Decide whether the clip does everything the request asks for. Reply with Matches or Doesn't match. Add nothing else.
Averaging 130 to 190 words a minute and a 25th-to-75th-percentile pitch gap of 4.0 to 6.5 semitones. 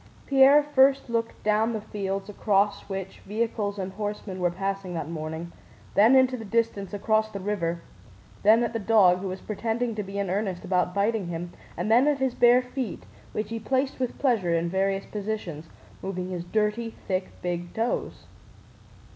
Doesn't match